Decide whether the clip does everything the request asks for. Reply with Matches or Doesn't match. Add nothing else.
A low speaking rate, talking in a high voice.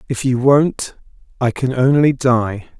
Doesn't match